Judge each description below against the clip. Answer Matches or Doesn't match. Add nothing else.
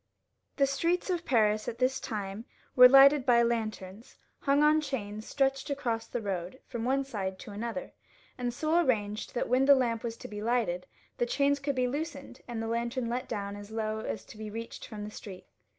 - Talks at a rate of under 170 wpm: Doesn't match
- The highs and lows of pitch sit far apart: Doesn't match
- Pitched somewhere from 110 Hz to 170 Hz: Doesn't match